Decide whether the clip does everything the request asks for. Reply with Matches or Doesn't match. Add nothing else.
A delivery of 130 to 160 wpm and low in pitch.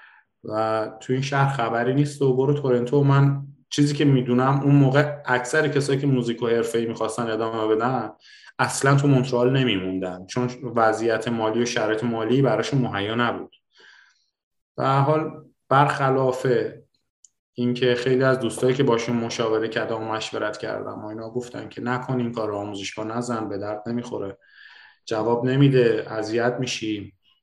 Matches